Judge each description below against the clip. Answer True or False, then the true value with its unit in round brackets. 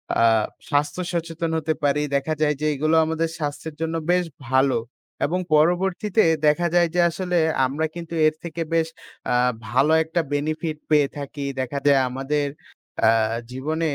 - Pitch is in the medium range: True (155 Hz)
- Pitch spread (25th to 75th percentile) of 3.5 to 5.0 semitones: False (2.7 semitones)